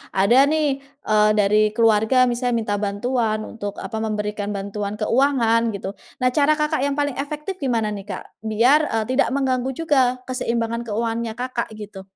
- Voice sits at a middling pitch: No, high, 230 Hz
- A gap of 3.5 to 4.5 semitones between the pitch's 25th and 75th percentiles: Yes, average, 3.9 semitones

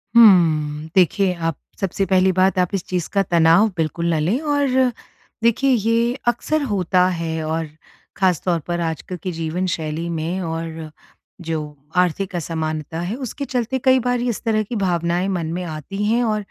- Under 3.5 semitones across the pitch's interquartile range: No, average, 4.5 semitones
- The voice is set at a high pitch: No, medium, 180 Hz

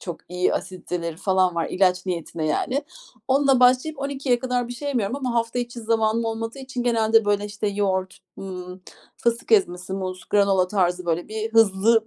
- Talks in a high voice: Yes, high, 215 Hz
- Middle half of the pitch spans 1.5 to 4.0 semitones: No, average, 4.6 semitones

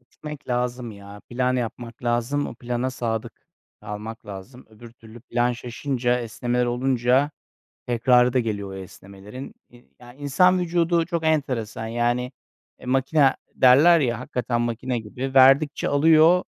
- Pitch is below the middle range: Yes, low, 125 Hz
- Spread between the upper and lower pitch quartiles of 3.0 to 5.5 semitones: No, narrow, 2.5 semitones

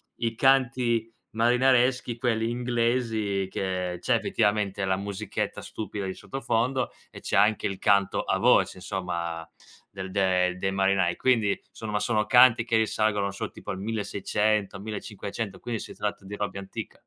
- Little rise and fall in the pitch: No, average, 3.2 semitones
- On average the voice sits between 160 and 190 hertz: No, low, 105 Hz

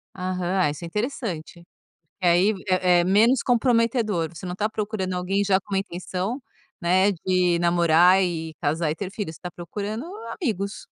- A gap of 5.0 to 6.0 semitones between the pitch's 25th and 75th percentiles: No, average, 3.2 semitones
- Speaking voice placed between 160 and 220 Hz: Yes, medium, 185 Hz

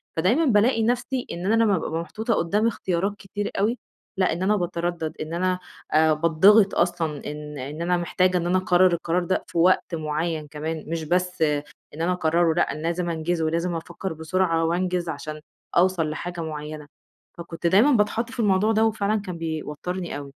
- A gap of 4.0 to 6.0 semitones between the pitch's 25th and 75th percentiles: No, average, 3.0 semitones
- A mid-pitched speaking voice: Yes, medium, 175 Hz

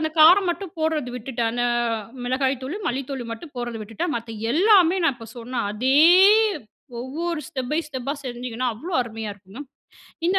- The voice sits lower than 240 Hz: No, very high, 260 Hz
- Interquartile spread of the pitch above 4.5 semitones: Yes, average, 4.9 semitones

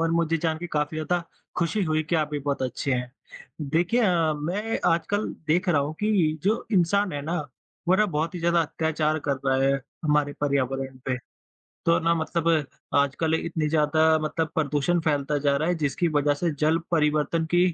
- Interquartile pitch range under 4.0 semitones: Yes, narrow, 2.5 semitones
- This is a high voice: No, medium, 160 Hz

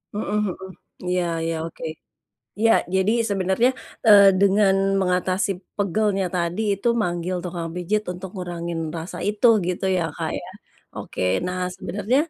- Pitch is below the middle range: No, high, 190 Hz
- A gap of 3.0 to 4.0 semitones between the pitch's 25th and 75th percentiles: No, narrow, 2.4 semitones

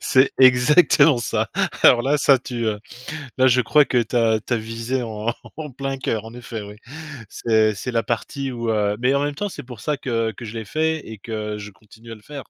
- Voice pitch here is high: No, low, 120 Hz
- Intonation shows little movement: No, average, 3.4 semitones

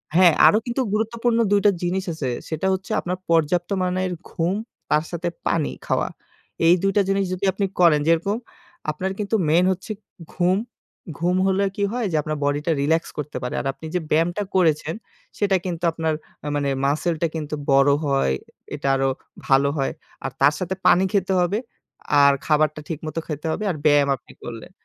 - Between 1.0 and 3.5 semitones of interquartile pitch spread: No, average, 3.9 semitones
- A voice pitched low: No, medium, 170 Hz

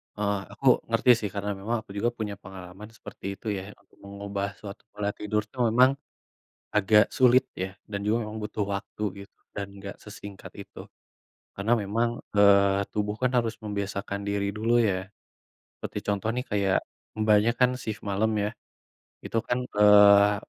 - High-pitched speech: No, low, 105 Hz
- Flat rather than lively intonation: Yes, narrow, 1.6 semitones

